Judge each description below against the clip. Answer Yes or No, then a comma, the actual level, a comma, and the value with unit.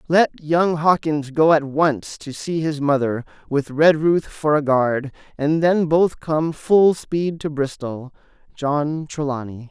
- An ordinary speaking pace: Yes, average, 155 wpm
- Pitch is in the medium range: Yes, medium, 150 Hz